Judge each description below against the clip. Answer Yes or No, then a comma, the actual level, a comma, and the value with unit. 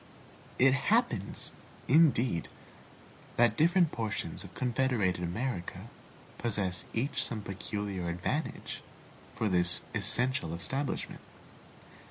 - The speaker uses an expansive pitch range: Yes, wide, 6.3 semitones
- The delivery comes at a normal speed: No, slow, 90 wpm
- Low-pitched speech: Yes, low, 115 Hz